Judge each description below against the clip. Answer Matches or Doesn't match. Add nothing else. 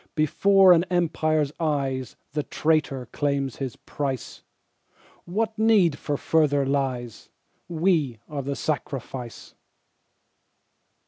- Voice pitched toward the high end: Doesn't match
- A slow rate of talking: Matches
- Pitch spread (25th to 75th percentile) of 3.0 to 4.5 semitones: Matches